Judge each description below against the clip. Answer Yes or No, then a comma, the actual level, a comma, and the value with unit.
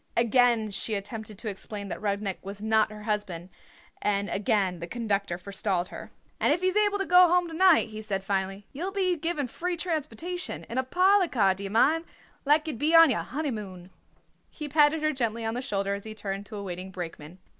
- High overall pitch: Yes, high, 220 Hz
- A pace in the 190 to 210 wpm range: Yes, fast, 205 wpm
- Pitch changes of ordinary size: No, wide, 7.7 semitones